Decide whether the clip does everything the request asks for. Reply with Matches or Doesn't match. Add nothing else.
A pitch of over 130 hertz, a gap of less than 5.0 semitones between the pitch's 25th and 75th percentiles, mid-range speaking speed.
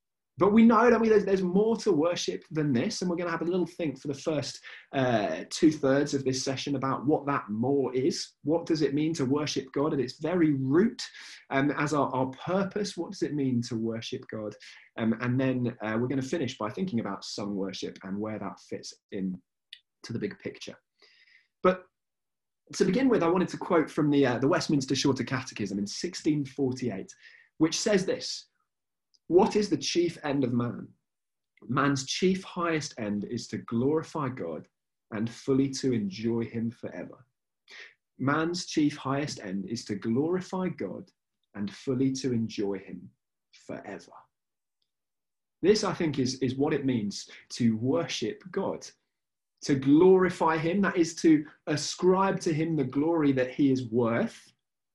Doesn't match